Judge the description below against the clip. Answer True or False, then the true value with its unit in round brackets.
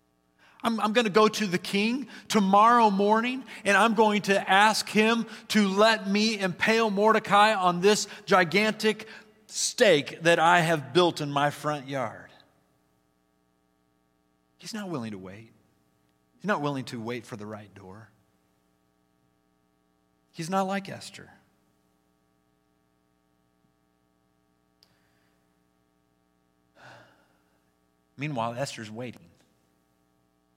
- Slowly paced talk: True (105 wpm)